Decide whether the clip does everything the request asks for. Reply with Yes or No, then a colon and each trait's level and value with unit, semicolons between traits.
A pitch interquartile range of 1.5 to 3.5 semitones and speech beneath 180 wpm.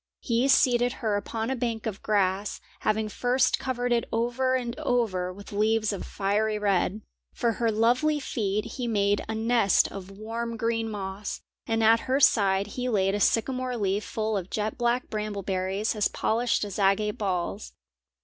Yes: average, 2.8 semitones; average, 170 wpm